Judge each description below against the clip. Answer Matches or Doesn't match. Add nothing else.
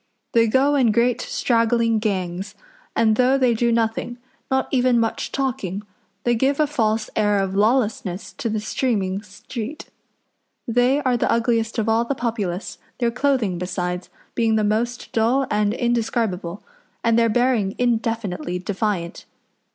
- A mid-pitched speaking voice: Doesn't match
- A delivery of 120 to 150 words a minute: Matches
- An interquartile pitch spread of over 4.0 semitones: Doesn't match